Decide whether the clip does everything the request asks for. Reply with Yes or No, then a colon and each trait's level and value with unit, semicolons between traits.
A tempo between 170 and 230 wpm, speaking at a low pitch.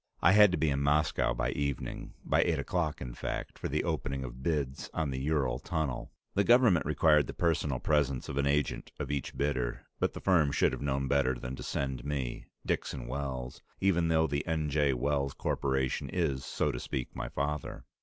Yes: average, 200 wpm; very low, 70 Hz